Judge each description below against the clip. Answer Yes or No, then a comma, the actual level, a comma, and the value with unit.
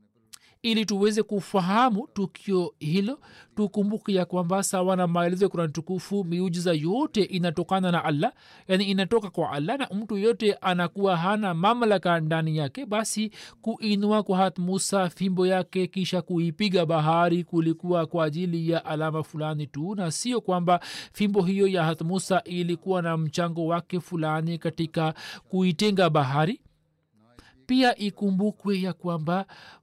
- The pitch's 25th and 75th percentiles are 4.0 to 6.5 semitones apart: No, average, 3.2 semitones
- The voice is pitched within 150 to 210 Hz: Yes, medium, 185 Hz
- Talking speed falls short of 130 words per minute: No, average, 135 wpm